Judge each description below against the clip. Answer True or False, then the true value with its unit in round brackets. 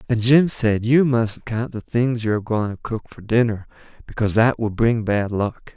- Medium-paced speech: False (220 wpm)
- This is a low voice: True (115 Hz)